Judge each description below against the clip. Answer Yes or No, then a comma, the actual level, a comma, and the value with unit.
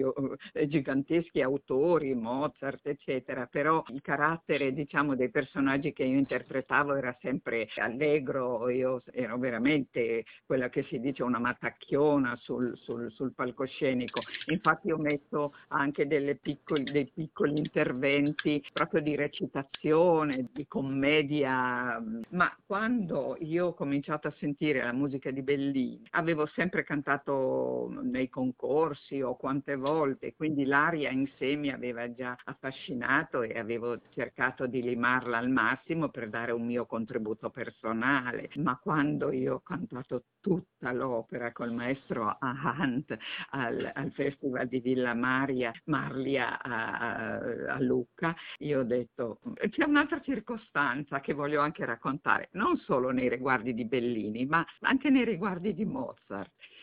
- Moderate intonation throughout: Yes, average, 3.3 semitones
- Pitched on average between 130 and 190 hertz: Yes, medium, 140 Hz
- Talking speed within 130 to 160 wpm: Yes, average, 135 wpm